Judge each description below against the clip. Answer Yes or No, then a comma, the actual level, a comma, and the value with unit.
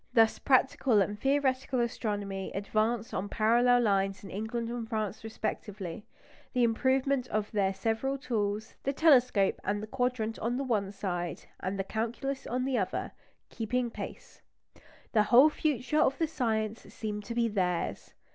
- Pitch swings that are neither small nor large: Yes, average, 3.5 semitones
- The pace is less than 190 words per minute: Yes, average, 155 wpm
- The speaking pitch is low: No, high, 225 Hz